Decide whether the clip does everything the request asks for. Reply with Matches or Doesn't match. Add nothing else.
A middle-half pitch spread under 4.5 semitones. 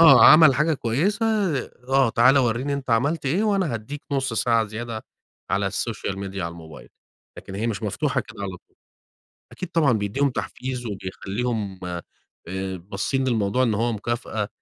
Doesn't match